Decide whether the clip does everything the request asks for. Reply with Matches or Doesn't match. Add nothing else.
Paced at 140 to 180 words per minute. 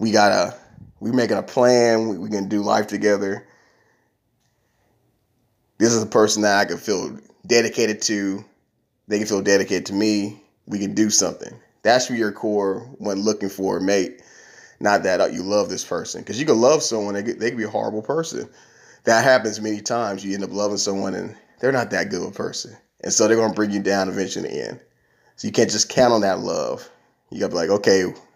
Doesn't match